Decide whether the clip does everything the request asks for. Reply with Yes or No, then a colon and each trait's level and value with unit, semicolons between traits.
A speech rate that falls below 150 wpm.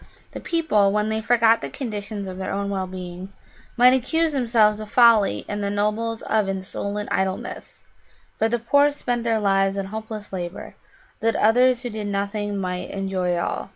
No: average, 175 wpm